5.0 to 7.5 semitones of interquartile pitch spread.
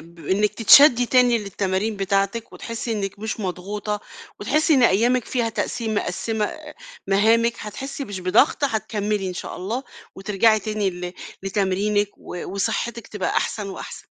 No: average, 2.9 semitones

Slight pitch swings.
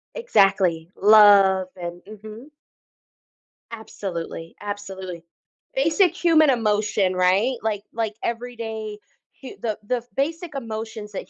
No: average, 3.7 semitones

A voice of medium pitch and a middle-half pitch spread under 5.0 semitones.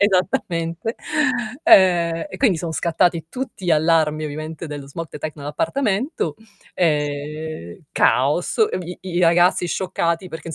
Yes: medium, 165 Hz; average, 2.7 semitones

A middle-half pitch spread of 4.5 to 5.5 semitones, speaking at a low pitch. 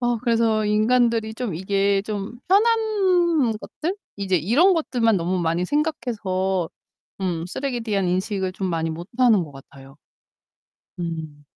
No: average, 5.1 semitones; high, 200 Hz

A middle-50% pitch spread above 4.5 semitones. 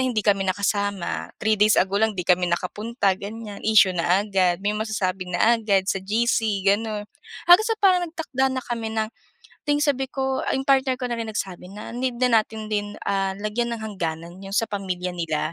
No: average, 3.7 semitones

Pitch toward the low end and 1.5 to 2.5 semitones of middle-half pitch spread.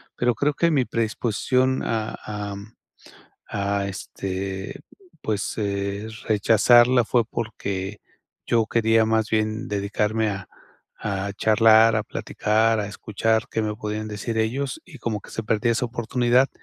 Yes: low, 110 Hz; narrow, 2.2 semitones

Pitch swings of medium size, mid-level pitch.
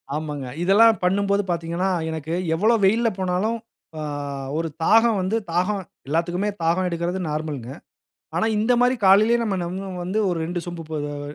Yes: average, 4.0 semitones; medium, 180 Hz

